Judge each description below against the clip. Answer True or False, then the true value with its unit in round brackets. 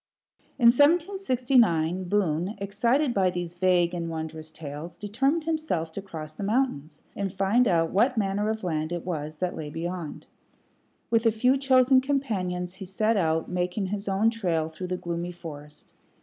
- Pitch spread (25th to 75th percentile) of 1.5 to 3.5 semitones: False (5.5 semitones)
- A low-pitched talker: False (185 Hz)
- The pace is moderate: True (165 wpm)